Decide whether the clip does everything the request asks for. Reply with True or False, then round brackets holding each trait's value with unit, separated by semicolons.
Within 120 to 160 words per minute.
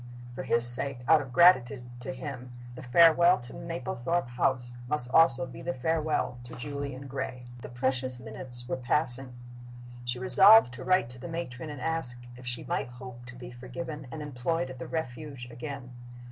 False (175 wpm)